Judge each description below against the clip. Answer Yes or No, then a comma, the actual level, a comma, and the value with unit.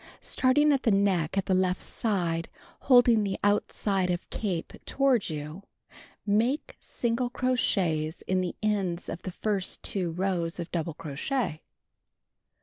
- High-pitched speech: Yes, high, 195 Hz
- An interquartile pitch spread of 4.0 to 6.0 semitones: Yes, average, 4.9 semitones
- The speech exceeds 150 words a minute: No, average, 140 wpm